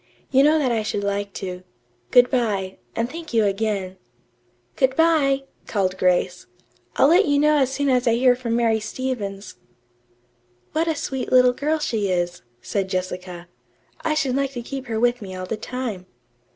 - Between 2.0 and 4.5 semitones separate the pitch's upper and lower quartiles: No, wide, 5.4 semitones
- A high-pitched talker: Yes, high, 240 Hz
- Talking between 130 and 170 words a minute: No, average, 180 wpm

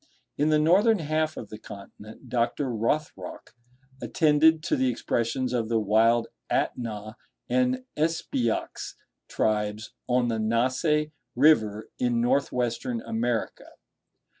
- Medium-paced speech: No, slow, 115 wpm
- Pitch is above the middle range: No, low, 120 Hz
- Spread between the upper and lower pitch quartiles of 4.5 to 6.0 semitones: Yes, average, 5.2 semitones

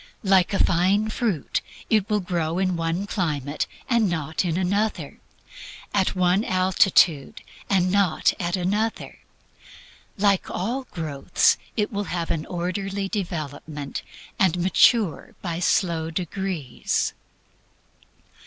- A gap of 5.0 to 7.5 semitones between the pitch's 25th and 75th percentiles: No, average, 3.2 semitones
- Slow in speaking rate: Yes, slow, 115 wpm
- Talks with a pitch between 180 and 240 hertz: Yes, medium, 185 Hz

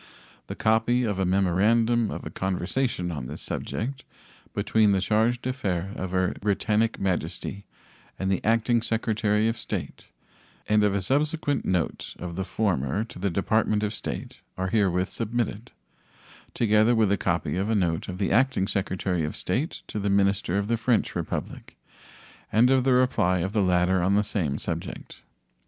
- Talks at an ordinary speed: Yes, average, 170 wpm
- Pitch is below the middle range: Yes, low, 105 Hz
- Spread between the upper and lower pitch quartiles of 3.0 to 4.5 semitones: Yes, average, 3.5 semitones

